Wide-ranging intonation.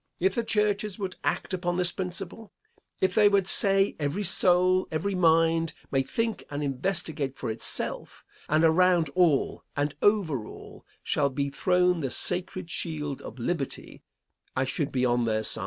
No: average, 4.8 semitones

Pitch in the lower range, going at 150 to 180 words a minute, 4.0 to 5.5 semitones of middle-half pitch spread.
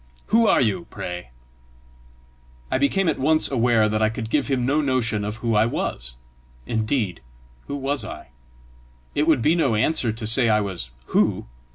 Yes: low, 115 Hz; average, 175 wpm; average, 4.8 semitones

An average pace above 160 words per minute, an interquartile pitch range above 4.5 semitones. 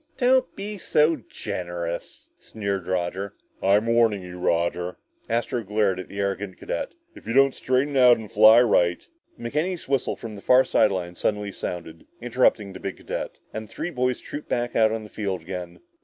Yes: average, 185 wpm; average, 5.2 semitones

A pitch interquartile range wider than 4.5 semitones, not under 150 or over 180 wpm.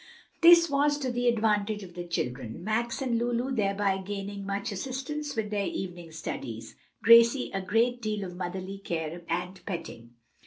Yes: average, 4.9 semitones; average, 160 wpm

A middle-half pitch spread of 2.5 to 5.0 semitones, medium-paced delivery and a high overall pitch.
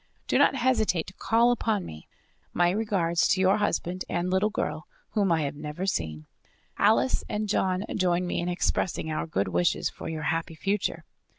No: average, 4.4 semitones; average, 180 wpm; medium, 180 Hz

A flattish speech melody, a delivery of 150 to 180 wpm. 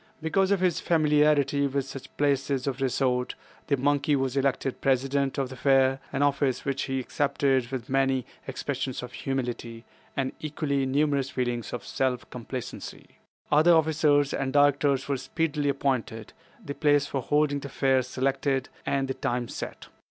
Yes: narrow, 1.7 semitones; average, 155 wpm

